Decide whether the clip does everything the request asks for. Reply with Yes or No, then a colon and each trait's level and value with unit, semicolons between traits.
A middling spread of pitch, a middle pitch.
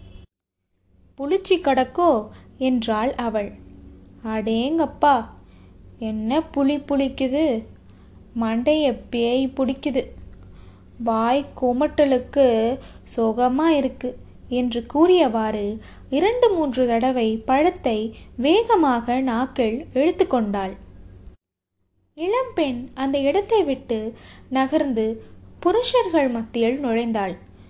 No: average, 4.5 semitones; very high, 250 Hz